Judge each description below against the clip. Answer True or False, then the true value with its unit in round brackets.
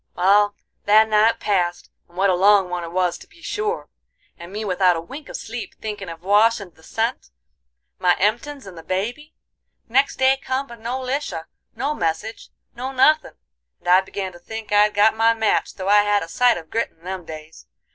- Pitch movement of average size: True (4.5 semitones)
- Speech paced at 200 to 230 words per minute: True (205 wpm)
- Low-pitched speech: False (205 Hz)